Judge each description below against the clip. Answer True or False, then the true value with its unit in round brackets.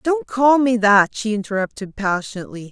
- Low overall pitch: False (210 Hz)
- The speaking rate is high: False (155 wpm)